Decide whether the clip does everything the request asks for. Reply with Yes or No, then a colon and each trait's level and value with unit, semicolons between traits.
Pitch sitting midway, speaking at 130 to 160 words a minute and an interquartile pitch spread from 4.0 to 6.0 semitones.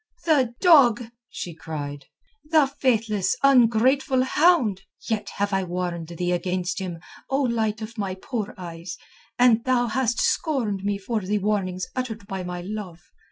No: high, 210 Hz; average, 150 wpm; average, 5.3 semitones